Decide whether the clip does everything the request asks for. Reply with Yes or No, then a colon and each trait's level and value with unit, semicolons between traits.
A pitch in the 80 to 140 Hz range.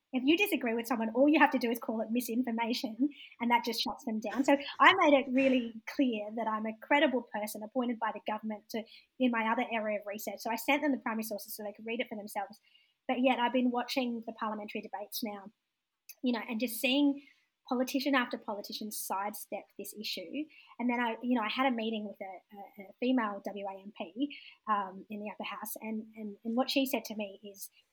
No: high, 230 Hz